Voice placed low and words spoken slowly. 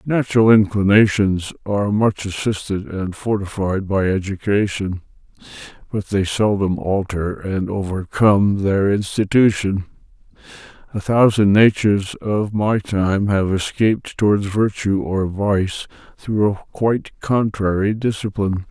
Yes: low, 100 Hz; slow, 110 wpm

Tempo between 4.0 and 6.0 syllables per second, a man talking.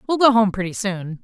No: 5.6 syllables/s; female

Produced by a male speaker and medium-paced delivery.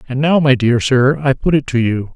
No: male; fast, 280 wpm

